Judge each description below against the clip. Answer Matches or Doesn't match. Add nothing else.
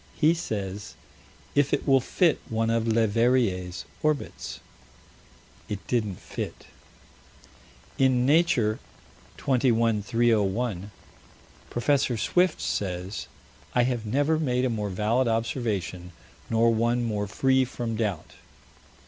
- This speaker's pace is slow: Matches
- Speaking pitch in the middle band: Doesn't match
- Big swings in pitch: Doesn't match